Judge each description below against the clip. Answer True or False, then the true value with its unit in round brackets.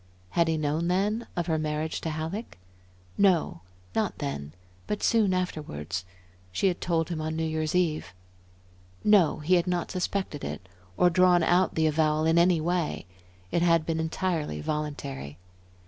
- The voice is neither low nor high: True (160 Hz)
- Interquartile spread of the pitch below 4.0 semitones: True (2.8 semitones)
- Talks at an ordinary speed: True (160 wpm)